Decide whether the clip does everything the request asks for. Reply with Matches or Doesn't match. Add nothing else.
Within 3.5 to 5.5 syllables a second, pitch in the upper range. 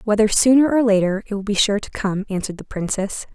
Doesn't match